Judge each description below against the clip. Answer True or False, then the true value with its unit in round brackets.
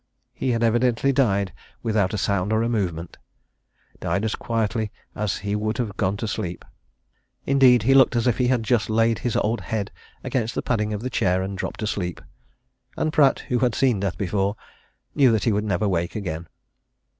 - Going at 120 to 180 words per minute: False (190 wpm)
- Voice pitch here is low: True (110 Hz)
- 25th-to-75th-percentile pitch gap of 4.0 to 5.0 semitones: False (3.2 semitones)